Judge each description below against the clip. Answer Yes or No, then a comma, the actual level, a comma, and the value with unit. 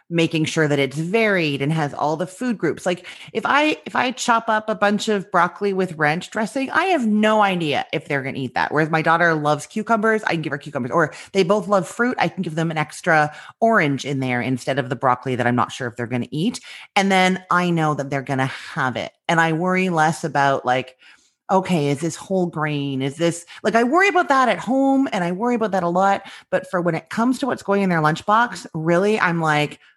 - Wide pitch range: Yes, wide, 5.8 semitones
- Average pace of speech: No, fast, 245 wpm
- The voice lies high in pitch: No, medium, 170 Hz